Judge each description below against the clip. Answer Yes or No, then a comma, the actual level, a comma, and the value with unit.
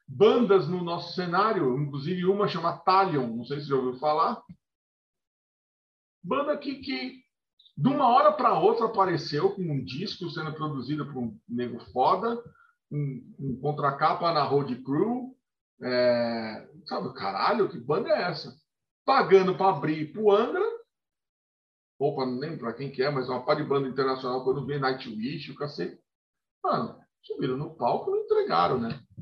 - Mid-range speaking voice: Yes, medium, 155 Hz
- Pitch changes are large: Yes, wide, 7.7 semitones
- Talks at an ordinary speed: Yes, average, 160 wpm